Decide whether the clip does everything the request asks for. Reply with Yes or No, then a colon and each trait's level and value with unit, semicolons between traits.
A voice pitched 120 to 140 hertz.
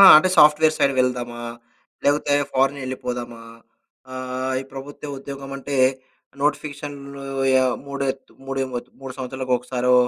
Yes: low, 135 Hz